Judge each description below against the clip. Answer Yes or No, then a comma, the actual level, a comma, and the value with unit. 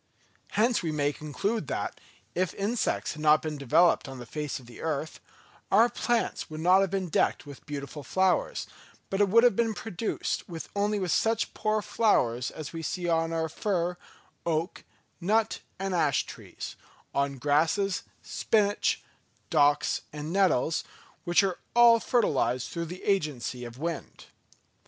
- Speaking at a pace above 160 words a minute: No, average, 150 wpm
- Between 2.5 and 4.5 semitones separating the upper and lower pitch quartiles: No, average, 5.2 semitones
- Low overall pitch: No, medium, 170 Hz